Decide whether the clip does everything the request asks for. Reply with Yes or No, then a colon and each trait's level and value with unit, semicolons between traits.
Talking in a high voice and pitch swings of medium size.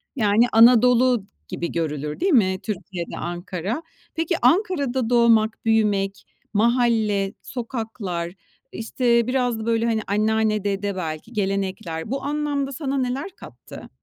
Yes: high, 225 Hz; average, 4.1 semitones